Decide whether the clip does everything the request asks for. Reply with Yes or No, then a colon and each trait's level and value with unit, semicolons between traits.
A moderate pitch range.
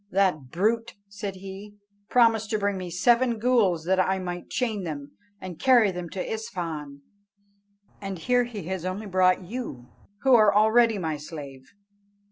Yes: average, 4.1 semitones